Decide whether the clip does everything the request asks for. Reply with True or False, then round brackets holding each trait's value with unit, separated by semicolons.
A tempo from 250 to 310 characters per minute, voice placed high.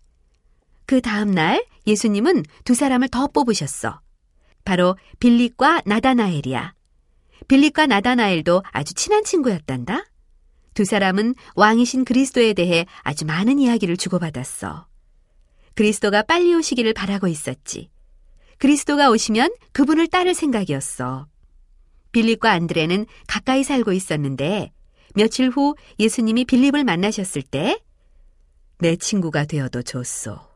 True (290 characters per minute; 205 Hz)